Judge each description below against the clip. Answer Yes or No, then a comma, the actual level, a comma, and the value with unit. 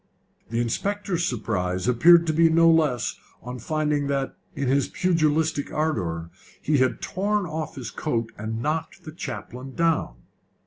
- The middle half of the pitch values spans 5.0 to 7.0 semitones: Yes, average, 5.3 semitones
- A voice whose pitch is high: No, medium, 150 Hz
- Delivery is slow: No, average, 145 wpm